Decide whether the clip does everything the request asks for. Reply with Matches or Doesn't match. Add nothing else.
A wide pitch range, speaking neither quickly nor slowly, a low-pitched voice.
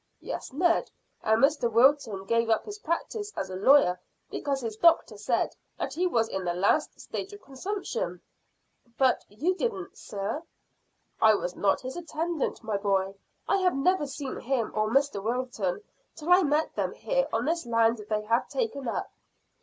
Doesn't match